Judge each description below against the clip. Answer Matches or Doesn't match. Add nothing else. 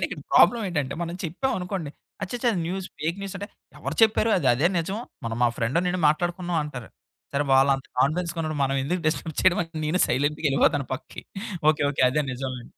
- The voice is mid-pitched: Matches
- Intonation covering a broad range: Doesn't match